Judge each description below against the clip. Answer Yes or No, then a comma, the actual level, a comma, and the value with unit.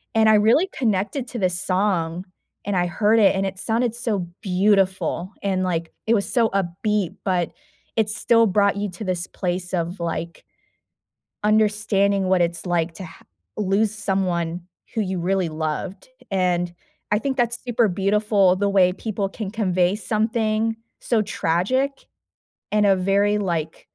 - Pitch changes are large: No, average, 3.0 semitones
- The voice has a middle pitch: No, high, 195 Hz